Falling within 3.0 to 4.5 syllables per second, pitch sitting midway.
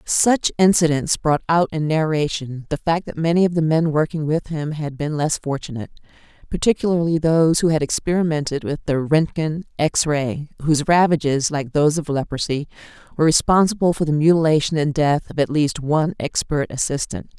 No: 5.5 syllables/s; medium, 155 Hz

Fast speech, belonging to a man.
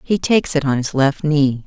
No: fast, 250 wpm; female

